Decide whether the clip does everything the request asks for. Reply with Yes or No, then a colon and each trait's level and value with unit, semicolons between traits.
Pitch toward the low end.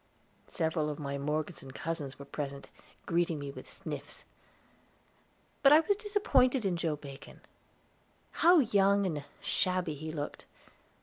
No: medium, 165 Hz